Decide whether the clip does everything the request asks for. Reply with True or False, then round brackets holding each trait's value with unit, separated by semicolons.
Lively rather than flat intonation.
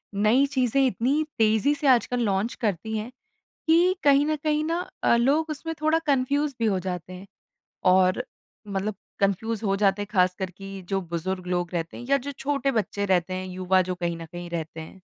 True (6.9 semitones)